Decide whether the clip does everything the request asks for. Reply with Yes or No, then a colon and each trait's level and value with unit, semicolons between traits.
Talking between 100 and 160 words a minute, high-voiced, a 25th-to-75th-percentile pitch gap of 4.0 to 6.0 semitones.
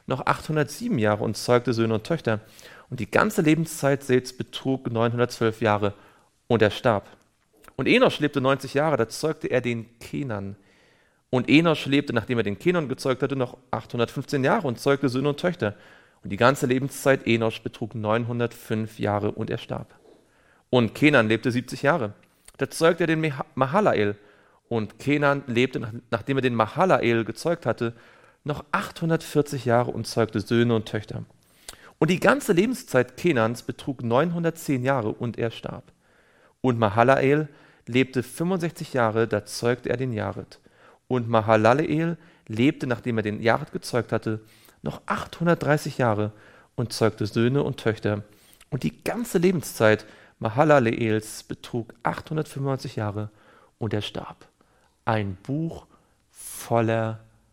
No: average, 140 wpm; low, 120 Hz; average, 4.4 semitones